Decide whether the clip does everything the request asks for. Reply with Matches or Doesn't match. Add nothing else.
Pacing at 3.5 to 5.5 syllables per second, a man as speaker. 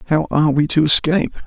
Doesn't match